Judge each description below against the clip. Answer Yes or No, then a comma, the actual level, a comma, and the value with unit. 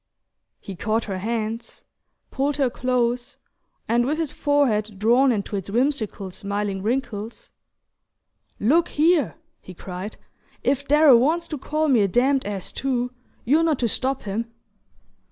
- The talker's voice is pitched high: Yes, high, 240 Hz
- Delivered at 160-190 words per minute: No, average, 140 wpm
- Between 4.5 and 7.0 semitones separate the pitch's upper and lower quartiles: Yes, average, 5.1 semitones